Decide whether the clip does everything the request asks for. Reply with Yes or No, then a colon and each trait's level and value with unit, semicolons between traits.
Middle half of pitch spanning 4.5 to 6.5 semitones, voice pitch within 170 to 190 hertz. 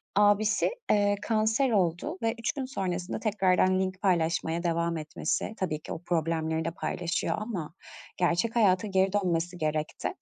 No: average, 3.8 semitones; medium, 185 Hz